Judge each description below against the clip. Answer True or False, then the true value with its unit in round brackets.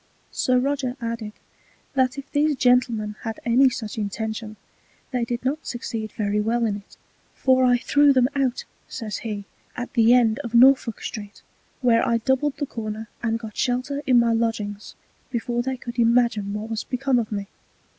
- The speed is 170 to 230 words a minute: True (175 wpm)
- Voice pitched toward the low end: False (235 Hz)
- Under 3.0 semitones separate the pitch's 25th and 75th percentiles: True (2.6 semitones)